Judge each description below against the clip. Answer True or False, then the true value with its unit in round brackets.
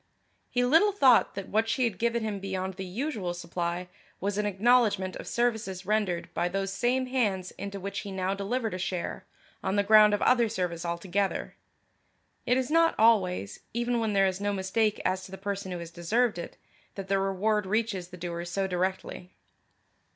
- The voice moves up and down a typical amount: True (3.3 semitones)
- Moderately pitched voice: False (195 Hz)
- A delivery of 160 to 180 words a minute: False (190 wpm)